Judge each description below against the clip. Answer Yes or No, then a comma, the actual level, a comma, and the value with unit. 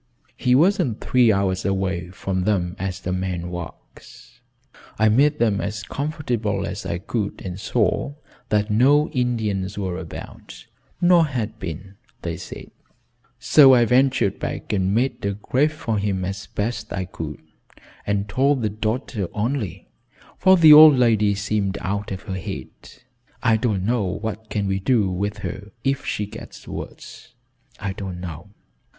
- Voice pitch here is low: Yes, low, 105 Hz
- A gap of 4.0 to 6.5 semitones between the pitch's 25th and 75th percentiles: Yes, average, 4.5 semitones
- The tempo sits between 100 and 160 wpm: Yes, average, 155 wpm